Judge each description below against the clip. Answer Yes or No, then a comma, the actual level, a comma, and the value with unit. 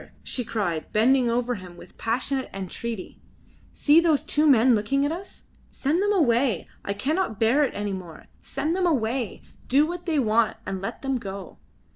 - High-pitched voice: Yes, high, 245 Hz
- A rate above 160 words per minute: Yes, average, 175 wpm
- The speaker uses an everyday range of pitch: No, wide, 5.8 semitones